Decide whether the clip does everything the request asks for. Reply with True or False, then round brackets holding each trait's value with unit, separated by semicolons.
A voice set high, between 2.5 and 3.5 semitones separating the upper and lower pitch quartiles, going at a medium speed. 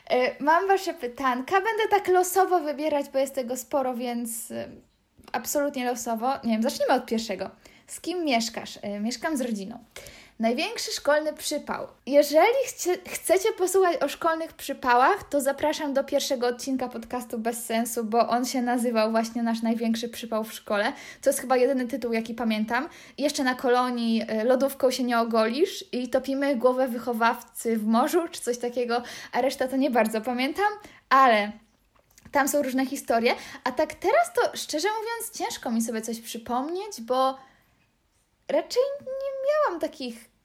False (260 Hz; 4.0 semitones; 150 wpm)